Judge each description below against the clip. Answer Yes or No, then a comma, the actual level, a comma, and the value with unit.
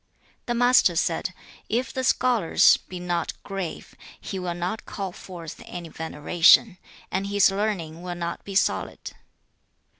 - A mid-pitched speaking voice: Yes, medium, 180 Hz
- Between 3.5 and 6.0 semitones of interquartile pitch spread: No, average, 2.9 semitones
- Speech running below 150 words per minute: Yes, average, 140 wpm